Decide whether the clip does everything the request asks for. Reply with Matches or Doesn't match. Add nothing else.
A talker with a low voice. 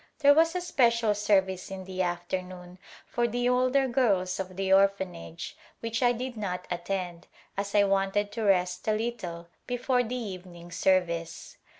Doesn't match